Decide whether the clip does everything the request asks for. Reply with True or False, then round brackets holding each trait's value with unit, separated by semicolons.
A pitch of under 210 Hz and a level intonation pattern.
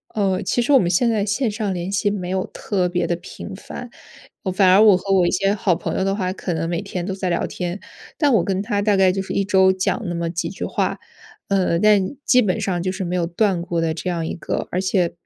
True (190 Hz; 2.3 semitones)